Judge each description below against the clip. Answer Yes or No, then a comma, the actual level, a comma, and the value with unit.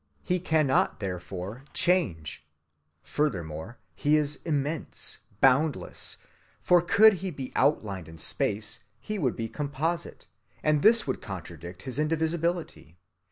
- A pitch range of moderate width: No, wide, 8.8 semitones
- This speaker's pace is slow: Yes, slow, 115 wpm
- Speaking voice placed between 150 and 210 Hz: No, medium, 140 Hz